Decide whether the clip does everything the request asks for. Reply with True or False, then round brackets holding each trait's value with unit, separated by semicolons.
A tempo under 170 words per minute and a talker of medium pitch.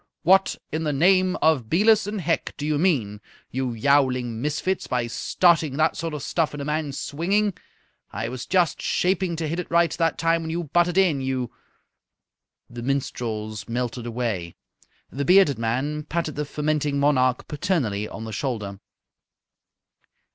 True (160 wpm; 150 Hz)